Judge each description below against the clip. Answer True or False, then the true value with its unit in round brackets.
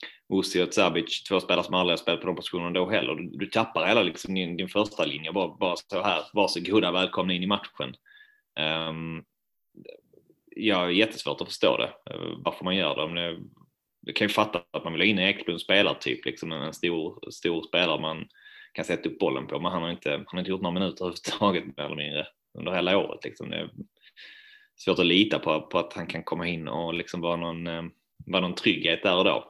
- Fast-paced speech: True (220 wpm)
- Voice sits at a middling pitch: False (90 Hz)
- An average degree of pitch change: True (3.7 semitones)